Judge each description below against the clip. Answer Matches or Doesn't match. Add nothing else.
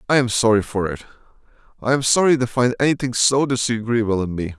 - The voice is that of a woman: Doesn't match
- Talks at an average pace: Matches